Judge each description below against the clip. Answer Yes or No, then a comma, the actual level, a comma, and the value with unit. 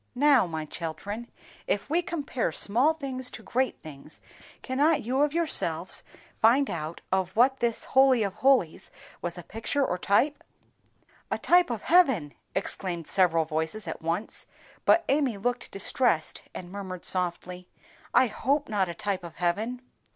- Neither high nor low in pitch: No, high, 215 Hz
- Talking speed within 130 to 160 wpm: Yes, average, 155 wpm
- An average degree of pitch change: No, wide, 7.1 semitones